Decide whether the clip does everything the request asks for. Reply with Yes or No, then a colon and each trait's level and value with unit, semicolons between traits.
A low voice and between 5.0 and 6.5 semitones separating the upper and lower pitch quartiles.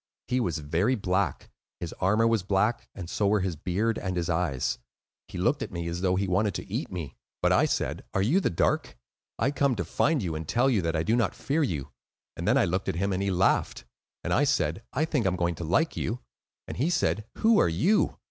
Yes: very low, 95 Hz; wide, 5.6 semitones